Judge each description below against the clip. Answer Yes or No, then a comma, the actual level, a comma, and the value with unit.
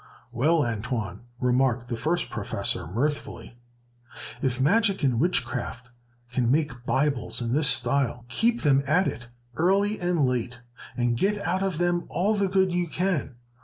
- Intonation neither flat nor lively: No, wide, 6.5 semitones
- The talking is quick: No, average, 150 wpm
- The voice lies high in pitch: No, medium, 140 Hz